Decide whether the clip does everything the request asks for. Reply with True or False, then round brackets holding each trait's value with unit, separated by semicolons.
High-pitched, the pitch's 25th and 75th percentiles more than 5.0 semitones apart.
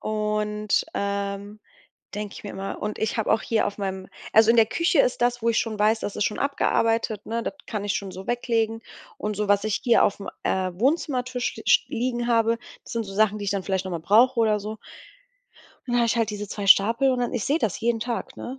False (220 Hz; 2.6 semitones)